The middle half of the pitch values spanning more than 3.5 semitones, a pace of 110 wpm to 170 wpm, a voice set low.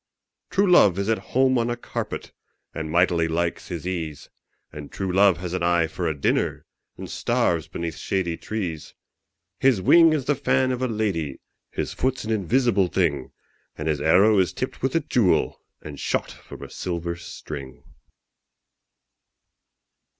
Yes: wide, 5.5 semitones; average, 160 wpm; very low, 90 Hz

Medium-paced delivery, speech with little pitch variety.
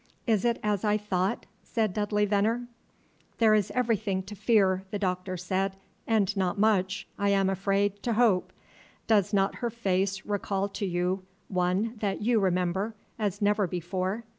Yes: average, 160 wpm; narrow, 2.2 semitones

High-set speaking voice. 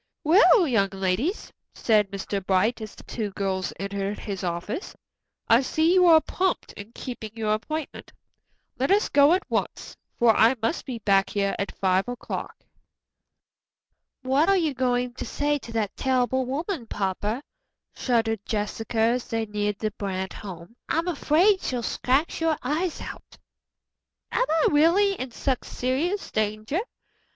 Yes: high, 240 Hz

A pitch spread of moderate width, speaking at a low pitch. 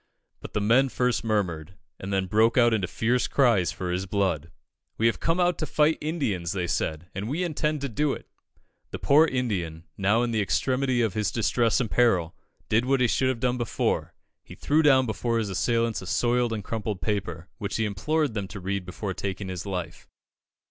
Yes: average, 4.9 semitones; low, 110 Hz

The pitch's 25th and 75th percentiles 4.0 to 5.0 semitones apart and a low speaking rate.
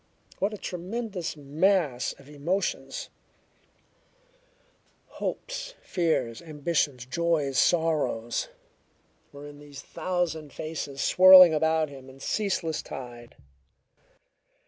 Yes: average, 4.3 semitones; slow, 90 wpm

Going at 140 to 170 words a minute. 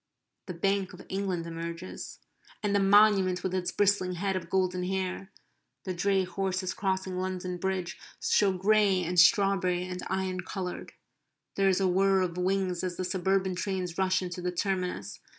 Yes: average, 165 wpm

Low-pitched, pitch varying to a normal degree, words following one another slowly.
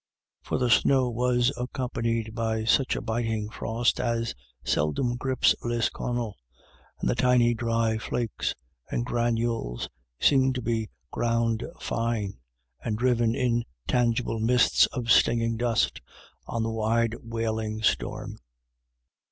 No: low, 115 Hz; narrow, 1.4 semitones; slow, 120 wpm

